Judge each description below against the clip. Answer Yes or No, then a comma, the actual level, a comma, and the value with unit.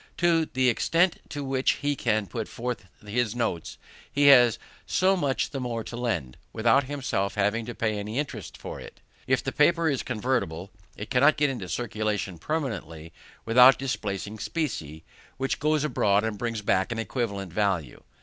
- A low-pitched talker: Yes, low, 120 Hz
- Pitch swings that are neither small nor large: Yes, average, 4.9 semitones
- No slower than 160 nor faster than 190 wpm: Yes, average, 170 wpm